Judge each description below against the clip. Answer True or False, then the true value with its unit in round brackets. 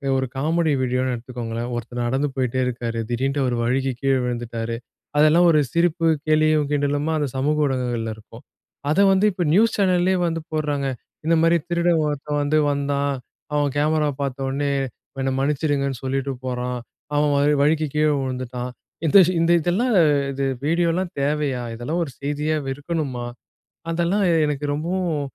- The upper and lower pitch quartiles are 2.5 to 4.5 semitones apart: True (3.6 semitones)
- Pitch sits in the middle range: True (145 Hz)